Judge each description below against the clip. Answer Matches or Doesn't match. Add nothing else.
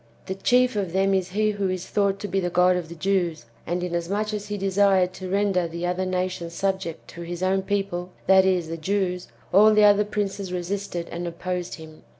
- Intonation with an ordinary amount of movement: Doesn't match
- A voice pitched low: Doesn't match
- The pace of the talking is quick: Matches